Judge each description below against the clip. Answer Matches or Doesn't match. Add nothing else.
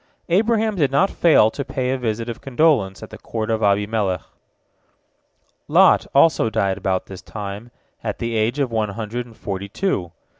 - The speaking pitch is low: Matches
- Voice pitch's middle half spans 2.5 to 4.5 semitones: Doesn't match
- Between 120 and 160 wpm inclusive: Doesn't match